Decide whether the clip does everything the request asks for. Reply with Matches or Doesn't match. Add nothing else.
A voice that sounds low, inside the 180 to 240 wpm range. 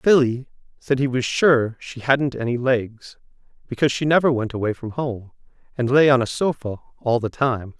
Matches